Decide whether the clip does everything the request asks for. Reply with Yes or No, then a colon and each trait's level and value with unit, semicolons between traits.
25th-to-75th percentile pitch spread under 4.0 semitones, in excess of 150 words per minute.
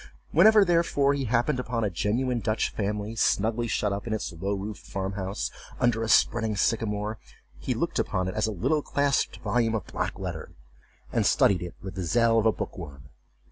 Yes: average, 3.4 semitones; average, 190 wpm